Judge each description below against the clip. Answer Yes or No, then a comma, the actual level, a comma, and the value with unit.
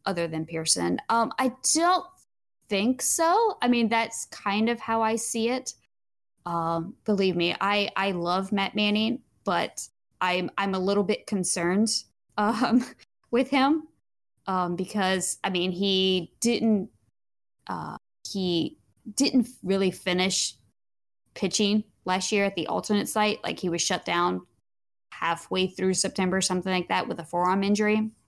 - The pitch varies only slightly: No, average, 4.0 semitones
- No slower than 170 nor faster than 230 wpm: No, average, 145 wpm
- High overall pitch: Yes, high, 195 Hz